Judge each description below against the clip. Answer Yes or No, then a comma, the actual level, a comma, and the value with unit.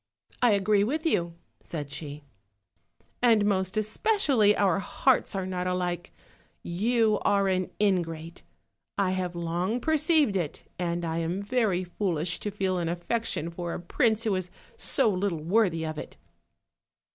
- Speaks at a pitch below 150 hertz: No, medium, 185 Hz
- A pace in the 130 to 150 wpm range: Yes, average, 145 wpm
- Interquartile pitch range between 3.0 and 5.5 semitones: Yes, average, 3.8 semitones